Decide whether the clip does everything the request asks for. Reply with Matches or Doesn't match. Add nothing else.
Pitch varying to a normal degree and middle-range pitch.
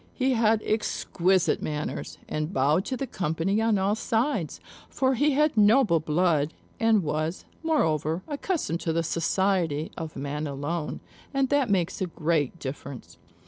Doesn't match